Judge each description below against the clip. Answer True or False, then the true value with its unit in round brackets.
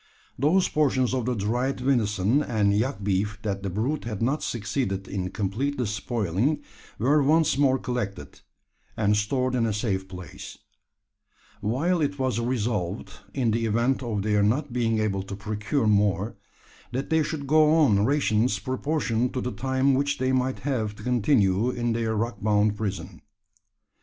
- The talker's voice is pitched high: False (115 Hz)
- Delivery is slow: False (160 wpm)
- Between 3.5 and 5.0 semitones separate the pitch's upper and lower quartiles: True (4.2 semitones)